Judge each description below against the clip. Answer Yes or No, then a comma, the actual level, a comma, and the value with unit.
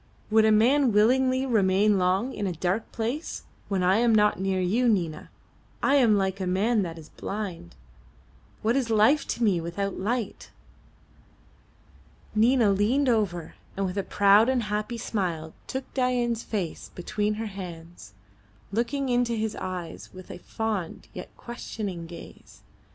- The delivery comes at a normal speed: Yes, average, 150 wpm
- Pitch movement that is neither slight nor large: Yes, average, 4.1 semitones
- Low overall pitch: No, high, 210 Hz